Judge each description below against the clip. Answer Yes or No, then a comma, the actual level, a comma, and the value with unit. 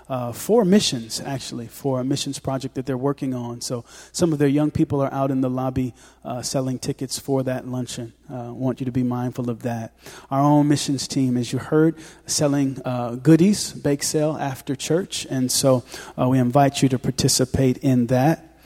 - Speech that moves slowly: No, average, 195 wpm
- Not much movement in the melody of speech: Yes, narrow, 2.2 semitones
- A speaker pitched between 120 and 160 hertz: Yes, low, 135 Hz